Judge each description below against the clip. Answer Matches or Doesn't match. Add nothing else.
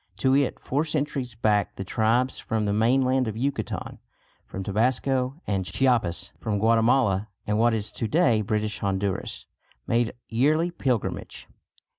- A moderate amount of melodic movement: Matches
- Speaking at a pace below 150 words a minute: Matches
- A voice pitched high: Doesn't match